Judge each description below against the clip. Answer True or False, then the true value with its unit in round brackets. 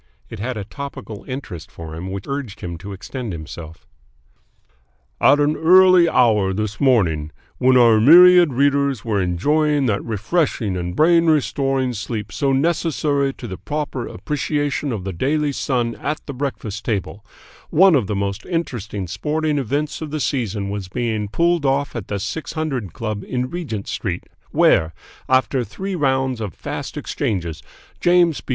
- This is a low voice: True (125 Hz)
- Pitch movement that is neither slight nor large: False (6.5 semitones)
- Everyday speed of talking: True (160 wpm)